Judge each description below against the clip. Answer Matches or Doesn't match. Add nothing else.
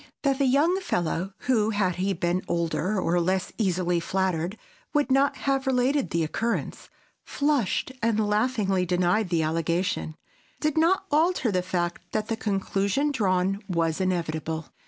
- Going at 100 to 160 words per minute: Matches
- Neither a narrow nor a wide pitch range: Doesn't match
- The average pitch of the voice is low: Doesn't match